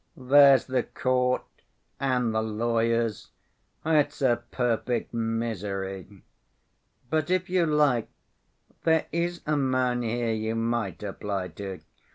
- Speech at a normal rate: No, slow, 110 wpm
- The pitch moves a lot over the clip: No, average, 3.8 semitones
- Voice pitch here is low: Yes, low, 120 Hz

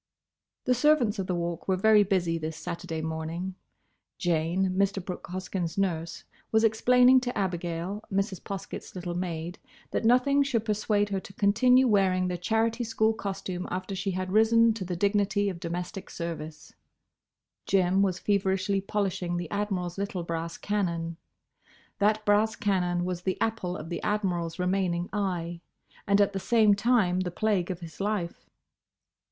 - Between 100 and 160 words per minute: Yes, average, 155 wpm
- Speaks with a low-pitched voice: No, high, 190 Hz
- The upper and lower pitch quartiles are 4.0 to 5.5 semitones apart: No, average, 3.0 semitones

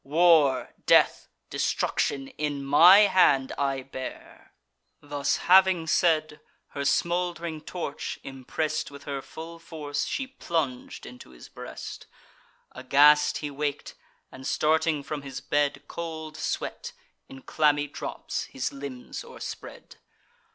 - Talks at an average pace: No, slow, 115 wpm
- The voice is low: No, medium, 145 Hz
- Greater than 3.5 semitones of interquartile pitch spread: No, average, 2.8 semitones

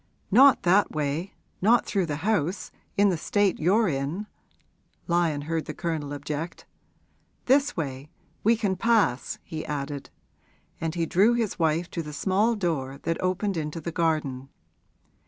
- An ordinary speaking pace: Yes, average, 150 wpm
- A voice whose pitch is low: No, medium, 170 Hz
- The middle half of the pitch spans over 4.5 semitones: Yes, average, 5.1 semitones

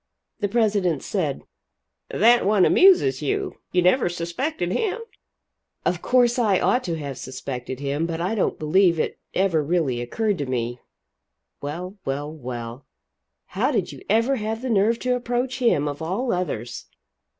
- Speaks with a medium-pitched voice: Yes, medium, 180 Hz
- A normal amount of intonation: No, wide, 7.9 semitones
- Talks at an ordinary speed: Yes, average, 155 wpm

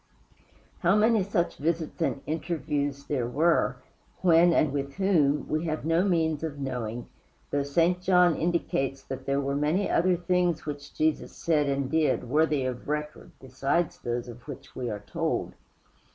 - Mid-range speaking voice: Yes, medium, 150 Hz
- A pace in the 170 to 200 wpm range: No, average, 160 wpm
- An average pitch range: Yes, average, 3.6 semitones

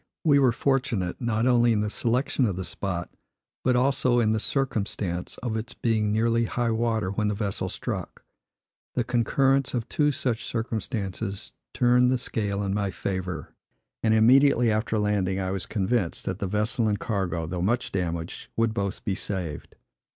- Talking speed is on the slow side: No, average, 170 wpm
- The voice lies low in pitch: Yes, low, 110 Hz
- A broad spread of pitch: No, average, 3.8 semitones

